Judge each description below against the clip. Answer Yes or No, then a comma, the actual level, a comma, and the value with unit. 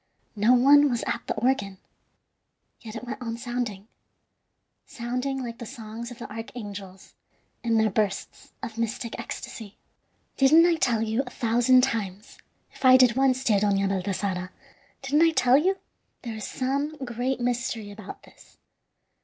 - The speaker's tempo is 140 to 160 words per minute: Yes, average, 155 wpm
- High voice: Yes, high, 235 Hz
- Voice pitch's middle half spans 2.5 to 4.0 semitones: Yes, average, 3.3 semitones